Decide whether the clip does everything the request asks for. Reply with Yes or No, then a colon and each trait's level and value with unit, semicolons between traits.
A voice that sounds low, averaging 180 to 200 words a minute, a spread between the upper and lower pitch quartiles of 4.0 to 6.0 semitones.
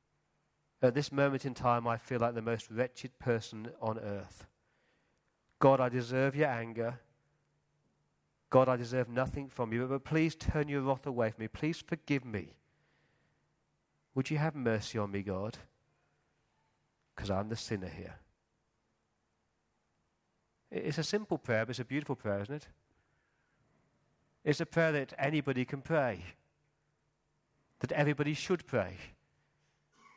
No: low, 130 Hz; average, 140 wpm; average, 4.3 semitones